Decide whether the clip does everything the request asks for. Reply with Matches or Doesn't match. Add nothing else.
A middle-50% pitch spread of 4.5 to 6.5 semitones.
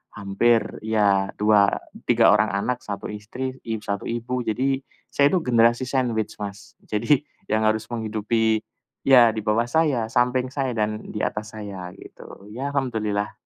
Doesn't match